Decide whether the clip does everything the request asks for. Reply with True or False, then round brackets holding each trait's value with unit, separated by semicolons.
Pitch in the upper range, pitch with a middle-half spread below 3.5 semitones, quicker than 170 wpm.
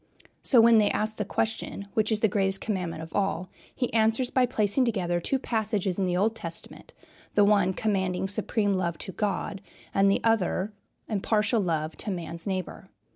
True (200 Hz; 3.0 semitones; 180 wpm)